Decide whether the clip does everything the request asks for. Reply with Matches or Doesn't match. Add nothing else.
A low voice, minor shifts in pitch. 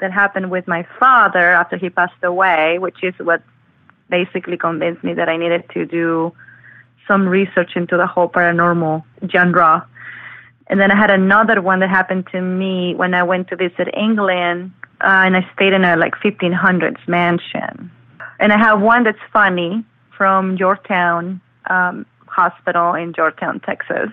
Doesn't match